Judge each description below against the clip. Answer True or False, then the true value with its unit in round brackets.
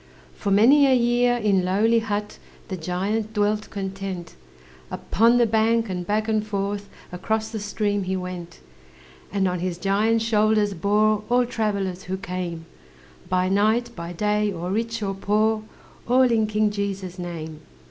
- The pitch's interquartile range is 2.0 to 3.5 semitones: True (2.8 semitones)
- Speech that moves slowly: False (155 wpm)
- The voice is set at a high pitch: True (205 Hz)